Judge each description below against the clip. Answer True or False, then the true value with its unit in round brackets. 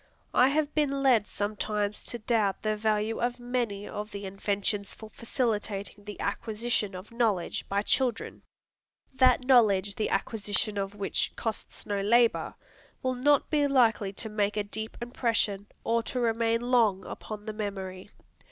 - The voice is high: True (215 Hz)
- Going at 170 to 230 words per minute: False (150 wpm)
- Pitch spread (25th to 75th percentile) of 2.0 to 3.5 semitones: True (2.9 semitones)